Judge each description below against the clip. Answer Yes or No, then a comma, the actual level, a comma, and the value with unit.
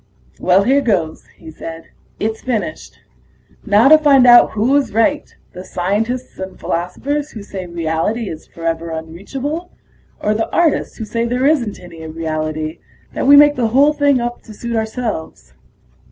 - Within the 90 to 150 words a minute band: No, average, 160 wpm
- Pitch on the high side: Yes, high, 220 Hz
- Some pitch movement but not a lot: No, wide, 7.6 semitones